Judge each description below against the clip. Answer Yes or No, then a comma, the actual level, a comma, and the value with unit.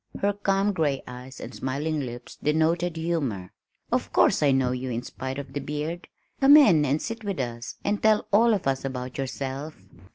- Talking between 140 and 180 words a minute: No, average, 190 wpm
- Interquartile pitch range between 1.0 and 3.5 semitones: No, average, 5.2 semitones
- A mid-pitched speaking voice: Yes, medium, 145 Hz